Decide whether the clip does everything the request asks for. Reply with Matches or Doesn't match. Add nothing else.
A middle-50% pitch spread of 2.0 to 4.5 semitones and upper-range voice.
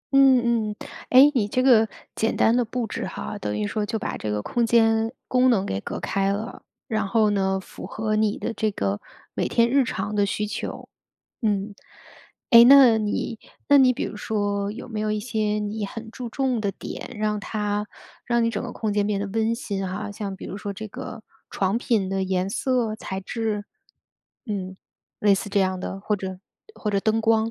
Matches